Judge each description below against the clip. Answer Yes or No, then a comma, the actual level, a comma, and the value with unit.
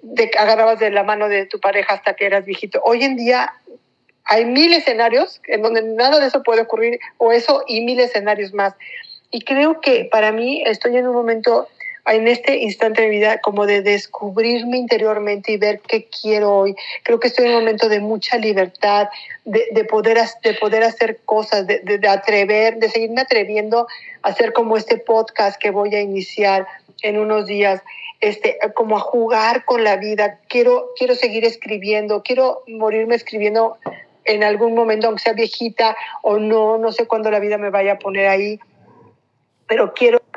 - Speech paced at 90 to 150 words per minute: No, average, 185 wpm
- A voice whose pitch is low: No, high, 225 Hz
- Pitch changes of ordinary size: No, narrow, 2.0 semitones